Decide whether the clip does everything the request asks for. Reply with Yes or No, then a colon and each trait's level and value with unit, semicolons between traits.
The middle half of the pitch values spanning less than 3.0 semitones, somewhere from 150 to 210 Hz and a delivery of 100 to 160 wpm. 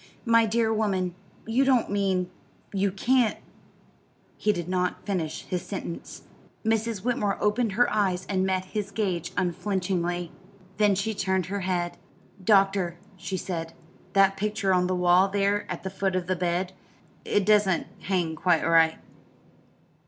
Yes: narrow, 2.6 semitones; high, 190 Hz; average, 150 wpm